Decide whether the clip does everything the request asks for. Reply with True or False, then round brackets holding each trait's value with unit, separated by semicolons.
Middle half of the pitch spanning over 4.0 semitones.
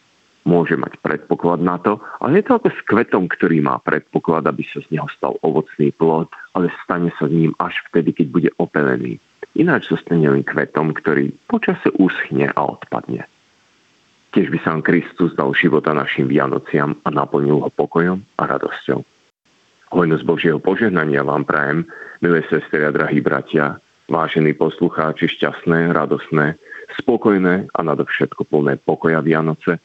False (2.8 semitones)